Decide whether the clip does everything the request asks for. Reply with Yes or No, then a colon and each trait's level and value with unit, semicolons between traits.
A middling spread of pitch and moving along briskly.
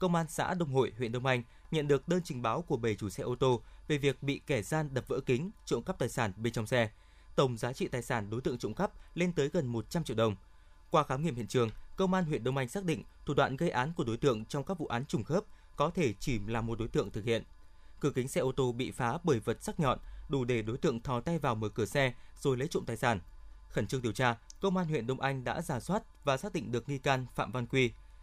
Yes: average, 4.6 semitones; fast, 275 wpm